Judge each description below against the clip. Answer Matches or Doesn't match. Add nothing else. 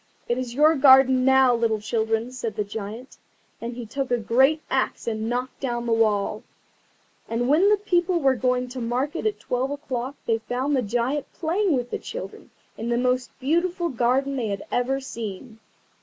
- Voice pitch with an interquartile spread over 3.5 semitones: Doesn't match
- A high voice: Matches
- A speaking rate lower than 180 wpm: Doesn't match